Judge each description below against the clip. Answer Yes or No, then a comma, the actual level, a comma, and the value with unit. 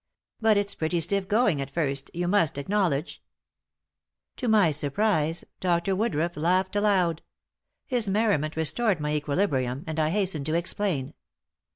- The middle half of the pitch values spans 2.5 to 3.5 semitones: No, average, 5.0 semitones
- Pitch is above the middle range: No, medium, 175 Hz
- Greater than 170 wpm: No, average, 140 wpm